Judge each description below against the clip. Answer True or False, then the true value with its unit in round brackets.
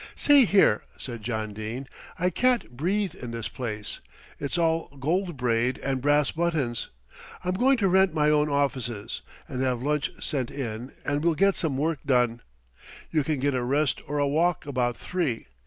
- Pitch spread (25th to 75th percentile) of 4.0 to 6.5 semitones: True (5.2 semitones)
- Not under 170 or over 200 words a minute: True (175 wpm)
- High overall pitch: False (145 Hz)